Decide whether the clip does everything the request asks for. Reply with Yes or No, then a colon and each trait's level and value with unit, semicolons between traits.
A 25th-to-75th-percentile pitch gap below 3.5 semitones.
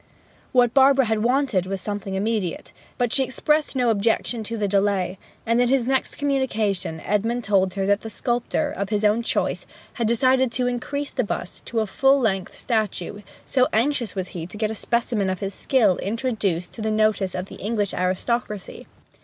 No: average, 3.8 semitones